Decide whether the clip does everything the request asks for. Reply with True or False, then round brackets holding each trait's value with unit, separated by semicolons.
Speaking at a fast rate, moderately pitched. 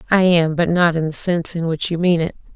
True (260 wpm; 170 Hz)